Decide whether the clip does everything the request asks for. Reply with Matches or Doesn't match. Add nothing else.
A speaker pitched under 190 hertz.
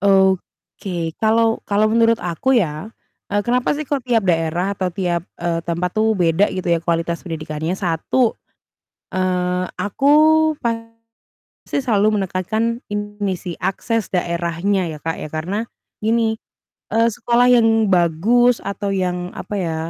Doesn't match